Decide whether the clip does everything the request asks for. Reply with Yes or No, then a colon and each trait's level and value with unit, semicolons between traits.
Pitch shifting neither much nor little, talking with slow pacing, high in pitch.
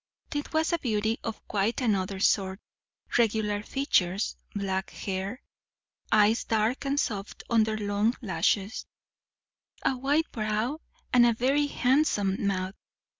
Yes: average, 4.0 semitones; slow, 125 wpm; high, 215 Hz